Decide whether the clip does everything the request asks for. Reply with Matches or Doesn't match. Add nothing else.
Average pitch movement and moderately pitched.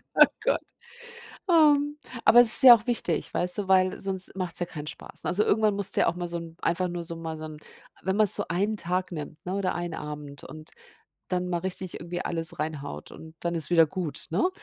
Matches